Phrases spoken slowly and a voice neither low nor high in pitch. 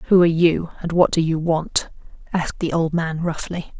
No: fast, 205 wpm; medium, 165 Hz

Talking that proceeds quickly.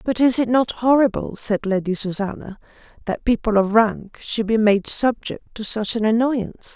No: average, 180 wpm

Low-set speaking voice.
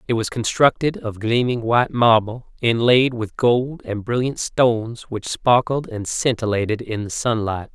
Yes: low, 115 Hz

